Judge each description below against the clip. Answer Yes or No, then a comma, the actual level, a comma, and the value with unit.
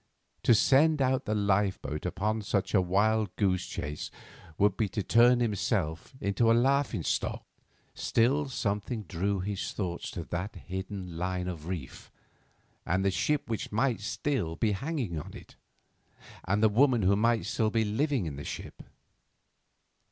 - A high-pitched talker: No, low, 105 Hz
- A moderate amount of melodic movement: Yes, average, 4.1 semitones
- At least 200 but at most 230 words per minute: No, average, 155 wpm